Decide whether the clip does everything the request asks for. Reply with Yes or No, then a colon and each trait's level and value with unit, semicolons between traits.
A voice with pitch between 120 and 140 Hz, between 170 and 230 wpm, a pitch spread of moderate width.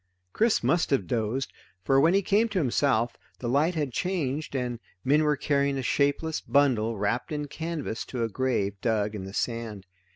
Yes: low, 135 Hz; average, 185 wpm; average, 4.8 semitones